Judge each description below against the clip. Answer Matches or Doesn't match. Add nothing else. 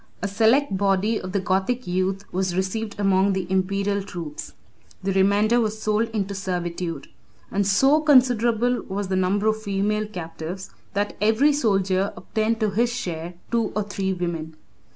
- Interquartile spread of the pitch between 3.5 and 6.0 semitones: Doesn't match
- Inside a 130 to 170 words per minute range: Matches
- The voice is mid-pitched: Doesn't match